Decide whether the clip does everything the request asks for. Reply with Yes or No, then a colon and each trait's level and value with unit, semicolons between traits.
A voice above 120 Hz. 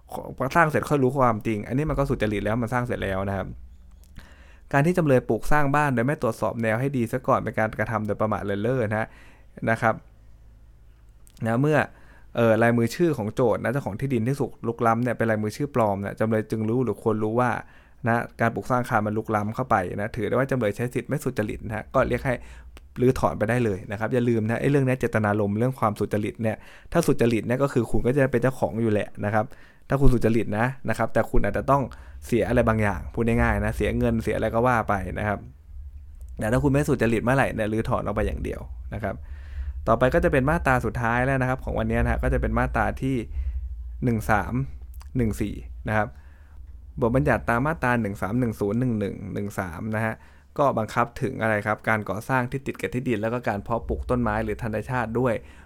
No: low, 110 Hz